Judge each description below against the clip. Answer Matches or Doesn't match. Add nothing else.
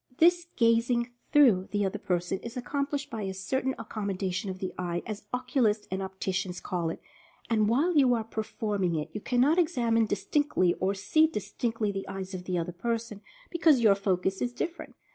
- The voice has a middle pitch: Doesn't match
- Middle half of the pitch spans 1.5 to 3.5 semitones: Doesn't match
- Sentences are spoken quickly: Doesn't match